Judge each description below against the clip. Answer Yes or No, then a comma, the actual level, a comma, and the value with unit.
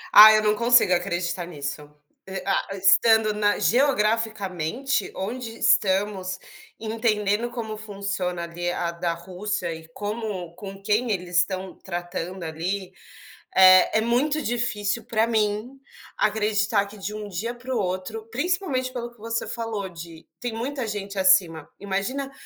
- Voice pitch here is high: Yes, high, 205 Hz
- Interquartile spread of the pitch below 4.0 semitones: Yes, average, 3.6 semitones